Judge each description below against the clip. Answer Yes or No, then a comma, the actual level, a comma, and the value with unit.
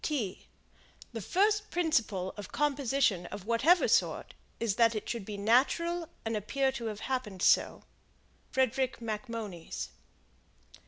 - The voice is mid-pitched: No, high, 235 Hz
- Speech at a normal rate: No, slow, 120 wpm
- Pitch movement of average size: Yes, average, 4.8 semitones